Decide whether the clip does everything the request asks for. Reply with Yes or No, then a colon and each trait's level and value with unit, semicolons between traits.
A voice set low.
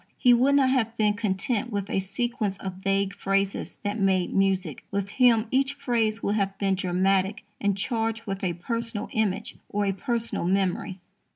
No: high, 200 Hz